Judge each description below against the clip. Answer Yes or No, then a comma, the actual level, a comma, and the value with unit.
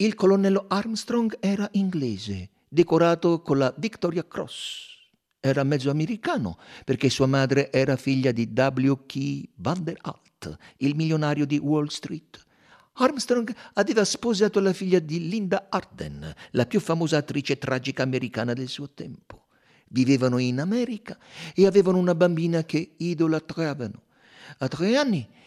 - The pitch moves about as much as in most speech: No, wide, 6.3 semitones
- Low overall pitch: No, medium, 155 Hz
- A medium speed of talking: Yes, average, 130 wpm